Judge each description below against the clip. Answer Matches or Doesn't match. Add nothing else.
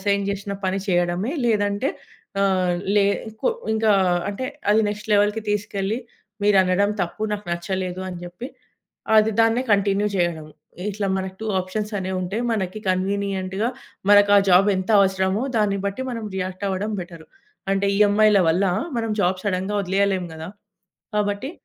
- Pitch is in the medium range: Doesn't match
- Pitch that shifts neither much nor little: Doesn't match